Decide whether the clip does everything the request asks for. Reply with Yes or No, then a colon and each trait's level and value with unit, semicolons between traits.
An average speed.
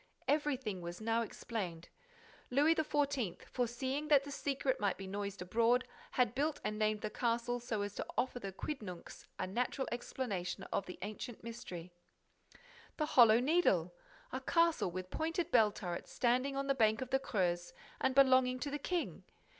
Yes: average, 165 wpm